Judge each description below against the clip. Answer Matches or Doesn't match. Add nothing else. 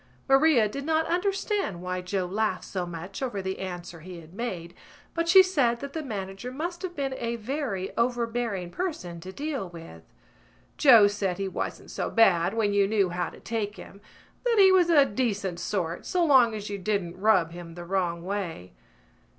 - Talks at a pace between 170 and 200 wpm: Matches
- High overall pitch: Matches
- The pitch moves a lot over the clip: Matches